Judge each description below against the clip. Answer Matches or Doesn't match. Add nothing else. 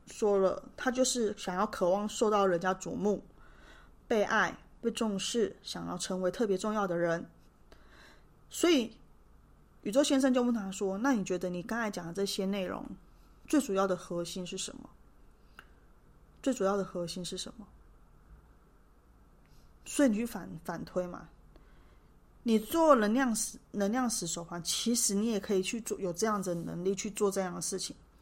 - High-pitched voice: Matches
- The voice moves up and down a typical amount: Matches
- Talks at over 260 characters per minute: Doesn't match